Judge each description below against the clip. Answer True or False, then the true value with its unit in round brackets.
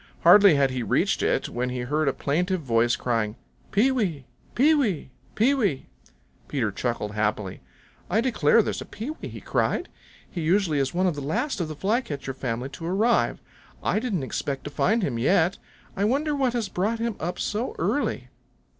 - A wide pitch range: True (8.8 semitones)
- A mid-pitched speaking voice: True (170 Hz)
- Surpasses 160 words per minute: True (180 wpm)